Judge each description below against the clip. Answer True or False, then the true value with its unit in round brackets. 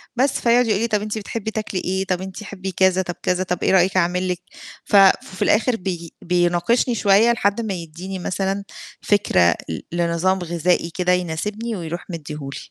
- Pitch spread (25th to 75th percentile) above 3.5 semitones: False (3.0 semitones)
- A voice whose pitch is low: False (185 Hz)